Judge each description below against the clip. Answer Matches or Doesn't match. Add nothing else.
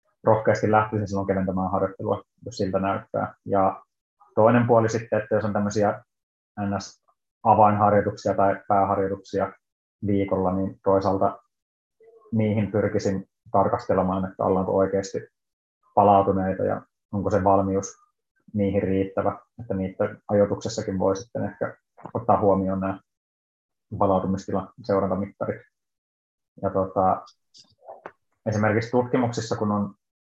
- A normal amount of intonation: Doesn't match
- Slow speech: Doesn't match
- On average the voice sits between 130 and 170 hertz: Doesn't match